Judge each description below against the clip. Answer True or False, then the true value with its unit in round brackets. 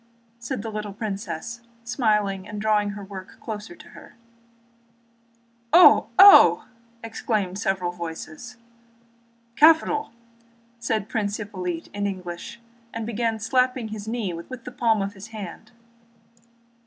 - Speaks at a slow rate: True (120 wpm)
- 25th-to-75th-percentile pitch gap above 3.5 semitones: False (2.9 semitones)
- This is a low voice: False (210 Hz)